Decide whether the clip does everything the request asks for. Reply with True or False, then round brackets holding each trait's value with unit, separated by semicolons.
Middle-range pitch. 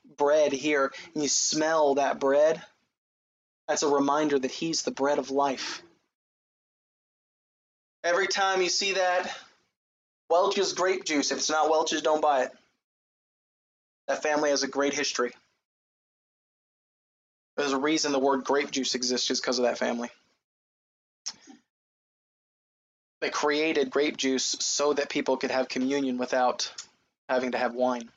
True (145 Hz)